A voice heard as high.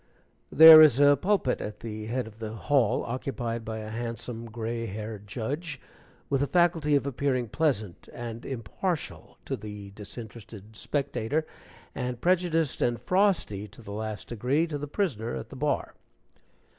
No: low, 120 Hz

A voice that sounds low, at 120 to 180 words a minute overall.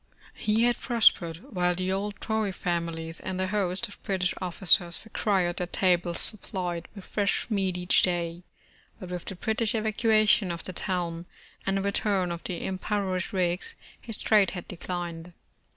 No: medium, 185 Hz; average, 160 wpm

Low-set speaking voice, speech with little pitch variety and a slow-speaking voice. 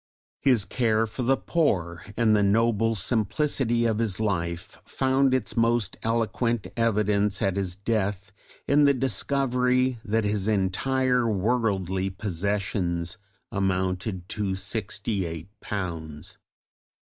No: low, 105 Hz; average, 3.8 semitones; slow, 115 wpm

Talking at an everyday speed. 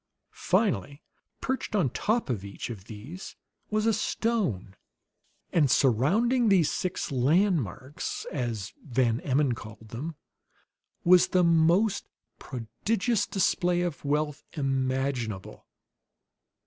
No: slow, 110 wpm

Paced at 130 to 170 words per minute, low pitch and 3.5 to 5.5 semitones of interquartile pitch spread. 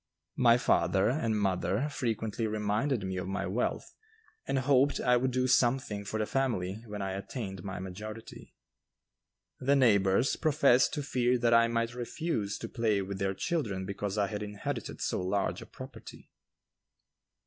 Yes: average, 160 wpm; low, 110 Hz; average, 4.2 semitones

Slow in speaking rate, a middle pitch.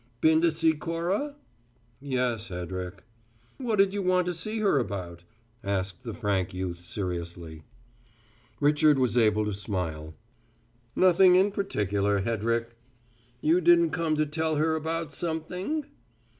Yes: slow, 130 wpm; medium, 145 Hz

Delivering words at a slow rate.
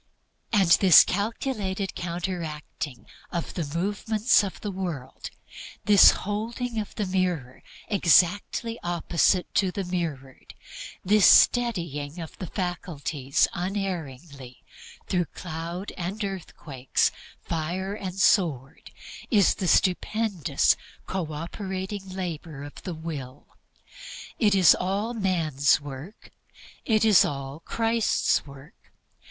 Yes: slow, 105 wpm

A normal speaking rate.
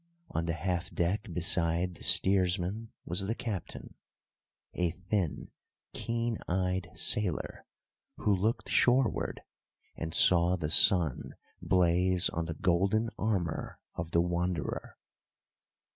No: slow, 115 wpm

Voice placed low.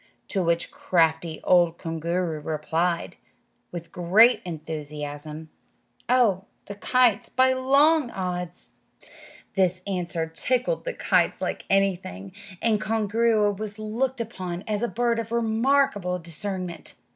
No: high, 190 Hz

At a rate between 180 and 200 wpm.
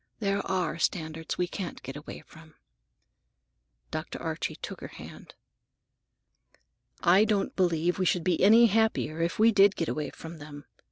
No: average, 155 wpm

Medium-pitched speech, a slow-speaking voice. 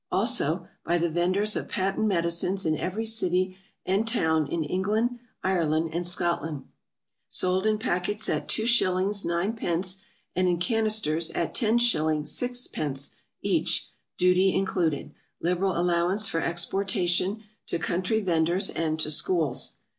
Yes: medium, 180 Hz; slow, 125 wpm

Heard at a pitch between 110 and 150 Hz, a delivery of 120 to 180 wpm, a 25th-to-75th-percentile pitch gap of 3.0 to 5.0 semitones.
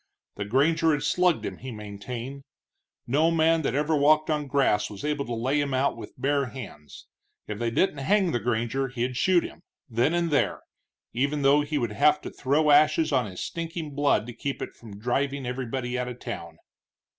No: medium, 140 Hz; average, 200 wpm; average, 3.8 semitones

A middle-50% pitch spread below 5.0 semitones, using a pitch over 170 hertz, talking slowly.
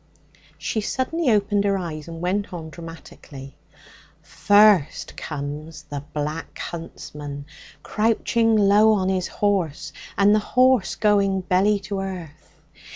Yes: average, 4.6 semitones; high, 190 Hz; slow, 120 wpm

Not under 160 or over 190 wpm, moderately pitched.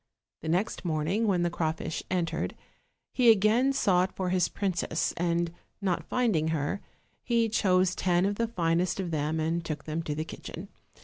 Yes: average, 170 wpm; medium, 180 Hz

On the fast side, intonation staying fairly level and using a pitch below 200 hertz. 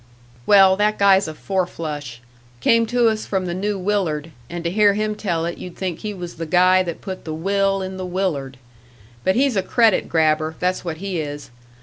No: fast, 210 wpm; average, 3.5 semitones; medium, 185 Hz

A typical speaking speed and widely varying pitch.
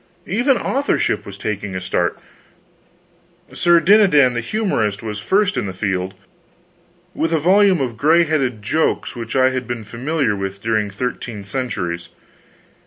Yes: average, 145 wpm; wide, 8.2 semitones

